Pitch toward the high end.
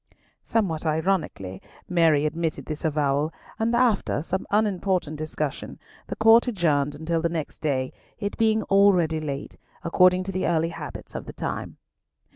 No: medium, 165 Hz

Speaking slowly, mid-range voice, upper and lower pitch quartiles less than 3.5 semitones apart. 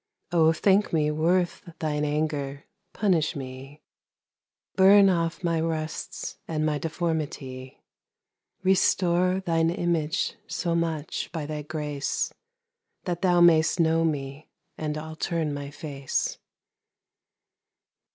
Yes: slow, 100 wpm; medium, 160 Hz; average, 2.8 semitones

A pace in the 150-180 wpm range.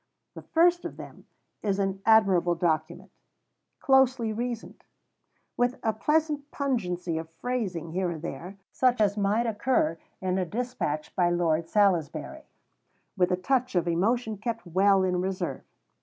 No: average, 140 wpm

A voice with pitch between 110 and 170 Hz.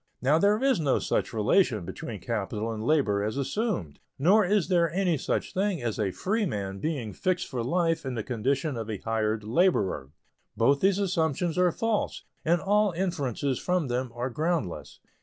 Yes: medium, 140 Hz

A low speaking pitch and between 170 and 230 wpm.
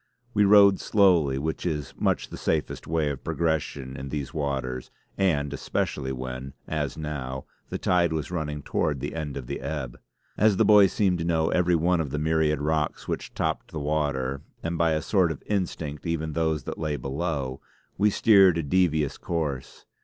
Yes: very low, 75 Hz; average, 185 wpm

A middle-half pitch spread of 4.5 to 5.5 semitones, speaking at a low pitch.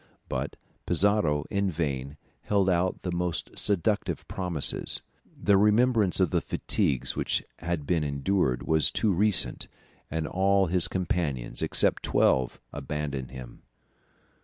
Yes: average, 5.2 semitones; very low, 85 Hz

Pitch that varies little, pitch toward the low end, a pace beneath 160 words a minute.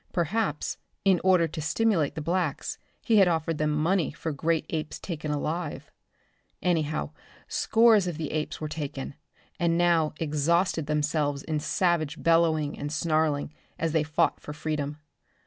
No: narrow, 2.2 semitones; medium, 160 Hz; average, 145 wpm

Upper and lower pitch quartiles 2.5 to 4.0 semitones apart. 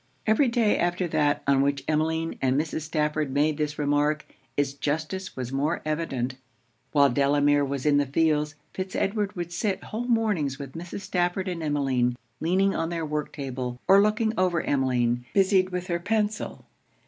No: average, 4.7 semitones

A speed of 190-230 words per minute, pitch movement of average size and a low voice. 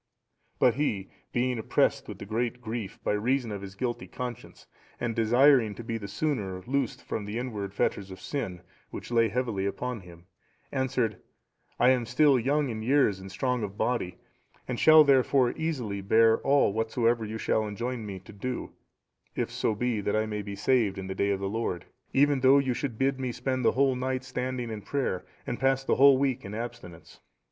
Yes: average, 195 wpm; average, 3.9 semitones; low, 120 Hz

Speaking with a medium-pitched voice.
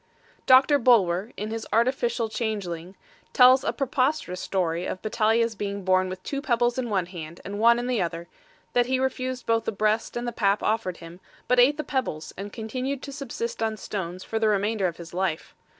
No: high, 220 Hz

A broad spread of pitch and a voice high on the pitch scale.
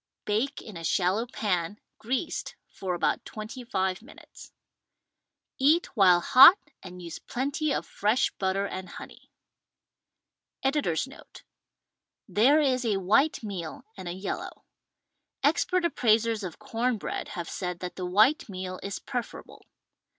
Yes: wide, 5.8 semitones; high, 210 Hz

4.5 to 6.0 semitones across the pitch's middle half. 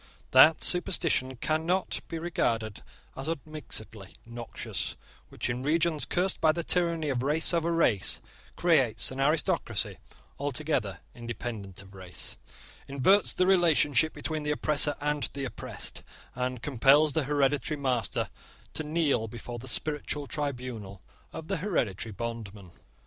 Yes: average, 5.1 semitones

